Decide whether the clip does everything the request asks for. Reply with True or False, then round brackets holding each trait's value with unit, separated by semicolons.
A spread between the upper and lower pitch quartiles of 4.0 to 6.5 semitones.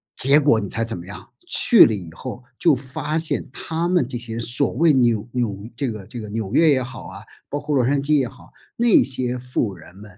True (4.4 semitones)